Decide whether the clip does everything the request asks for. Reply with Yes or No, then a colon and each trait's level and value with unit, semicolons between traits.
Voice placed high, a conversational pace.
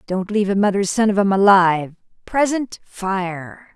Yes: high, 200 Hz; average, 160 wpm